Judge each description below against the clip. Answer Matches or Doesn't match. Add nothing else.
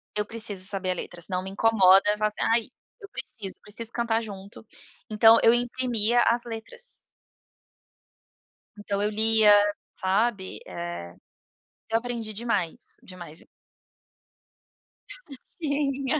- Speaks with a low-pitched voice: Doesn't match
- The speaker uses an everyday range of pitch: Matches